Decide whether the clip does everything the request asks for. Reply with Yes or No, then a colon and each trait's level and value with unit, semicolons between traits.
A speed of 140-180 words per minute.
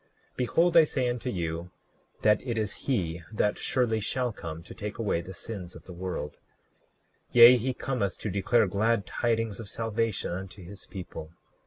Yes: average, 170 wpm